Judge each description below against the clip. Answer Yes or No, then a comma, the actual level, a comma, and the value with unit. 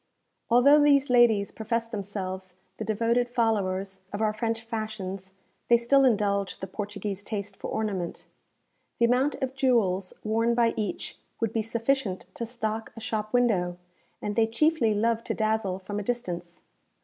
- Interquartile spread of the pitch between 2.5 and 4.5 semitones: Yes, average, 2.9 semitones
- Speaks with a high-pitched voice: Yes, high, 220 Hz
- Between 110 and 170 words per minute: Yes, average, 155 wpm